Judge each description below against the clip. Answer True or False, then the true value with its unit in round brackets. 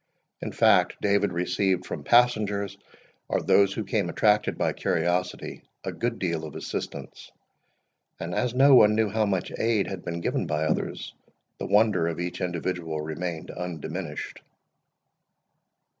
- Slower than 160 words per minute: True (145 wpm)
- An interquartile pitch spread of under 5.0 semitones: True (3.7 semitones)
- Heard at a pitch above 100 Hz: False (95 Hz)